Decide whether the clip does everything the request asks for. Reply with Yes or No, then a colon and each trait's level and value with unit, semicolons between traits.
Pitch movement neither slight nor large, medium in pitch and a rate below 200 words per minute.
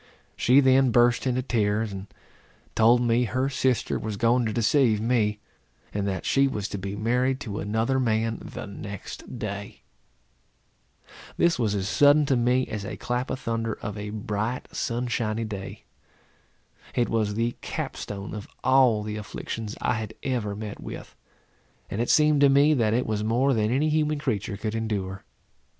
No: average, 3.4 semitones; low, 115 Hz; average, 170 wpm